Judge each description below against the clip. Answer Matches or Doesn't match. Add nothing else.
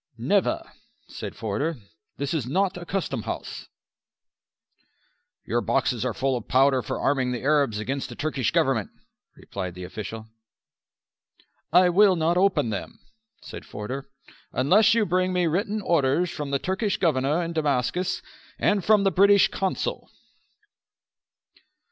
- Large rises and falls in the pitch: Matches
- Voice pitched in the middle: Matches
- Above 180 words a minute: Doesn't match